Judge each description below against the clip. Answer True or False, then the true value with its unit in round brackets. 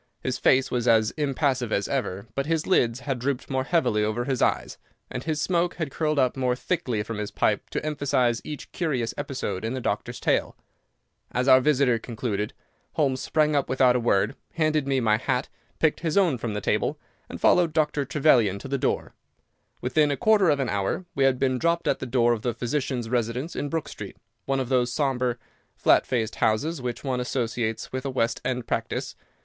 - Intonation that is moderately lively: True (3.7 semitones)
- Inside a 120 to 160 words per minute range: False (200 wpm)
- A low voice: True (130 Hz)